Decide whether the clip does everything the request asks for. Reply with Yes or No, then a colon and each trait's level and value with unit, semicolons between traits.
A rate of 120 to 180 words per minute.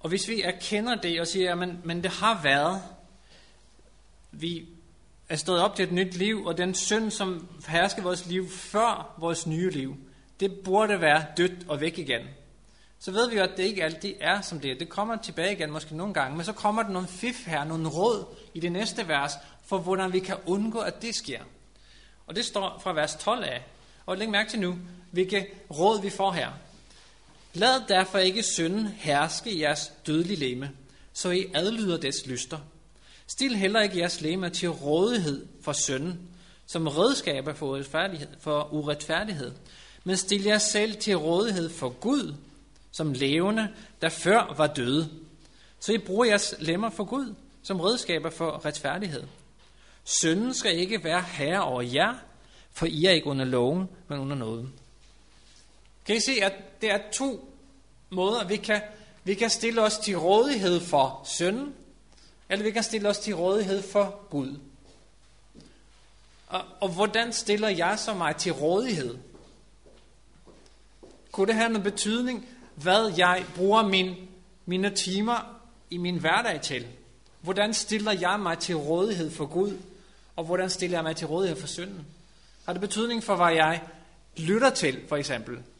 Yes: average, 170 wpm